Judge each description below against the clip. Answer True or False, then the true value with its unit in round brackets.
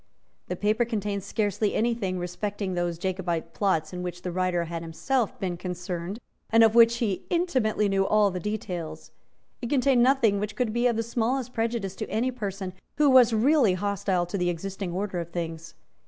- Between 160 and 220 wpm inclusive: True (185 wpm)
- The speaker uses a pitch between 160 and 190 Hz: False (200 Hz)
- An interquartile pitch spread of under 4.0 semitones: False (4.3 semitones)